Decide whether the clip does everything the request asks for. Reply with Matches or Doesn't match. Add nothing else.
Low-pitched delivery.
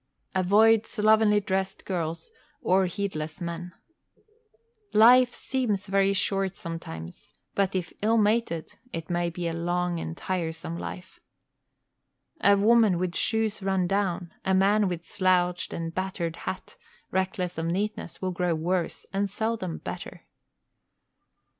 Doesn't match